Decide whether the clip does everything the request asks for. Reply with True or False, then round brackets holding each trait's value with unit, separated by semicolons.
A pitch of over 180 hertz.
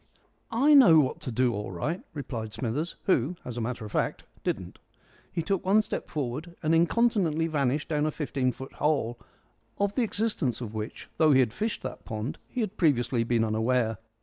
False (140 Hz)